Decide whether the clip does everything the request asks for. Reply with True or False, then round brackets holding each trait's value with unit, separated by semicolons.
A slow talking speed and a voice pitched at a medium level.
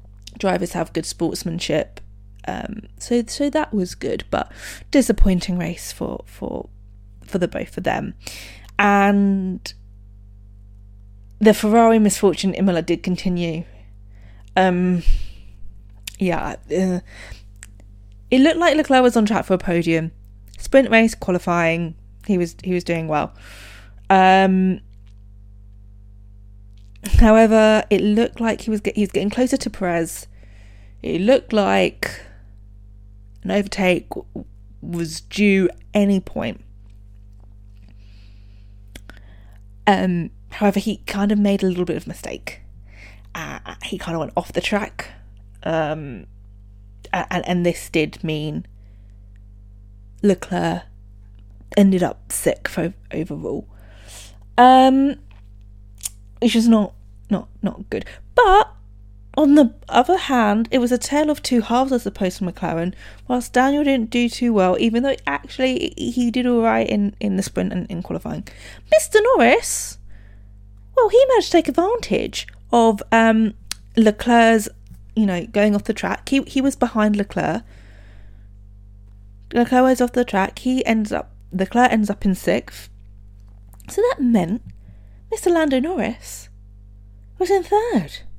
True (130 wpm; 170 Hz)